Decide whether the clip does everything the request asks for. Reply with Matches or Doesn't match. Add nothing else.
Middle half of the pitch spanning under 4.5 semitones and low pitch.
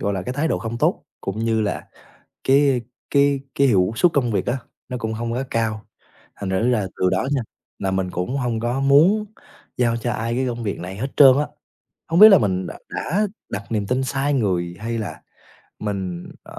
Doesn't match